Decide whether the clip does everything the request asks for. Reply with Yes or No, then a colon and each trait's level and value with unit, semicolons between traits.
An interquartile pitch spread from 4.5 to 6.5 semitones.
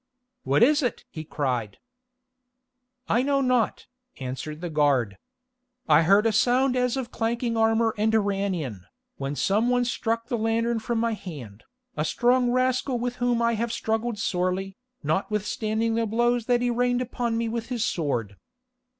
Yes: average, 4.8 semitones